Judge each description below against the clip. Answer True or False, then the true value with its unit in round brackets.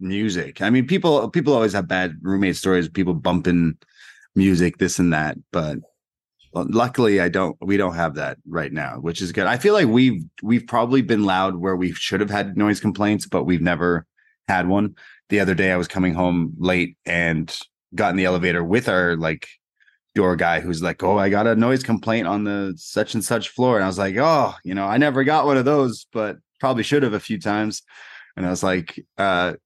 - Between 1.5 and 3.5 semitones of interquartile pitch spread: False (3.9 semitones)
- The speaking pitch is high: False (95 Hz)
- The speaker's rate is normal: False (215 wpm)